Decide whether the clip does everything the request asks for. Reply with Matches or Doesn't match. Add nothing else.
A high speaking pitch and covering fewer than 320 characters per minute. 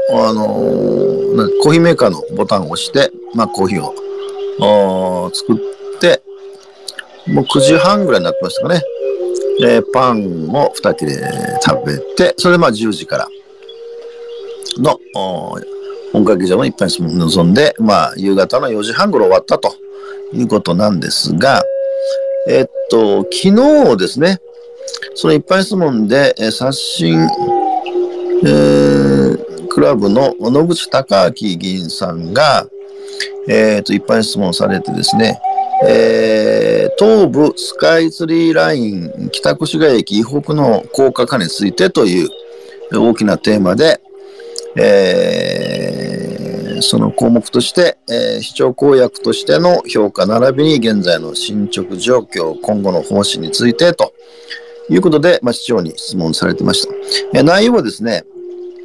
Matches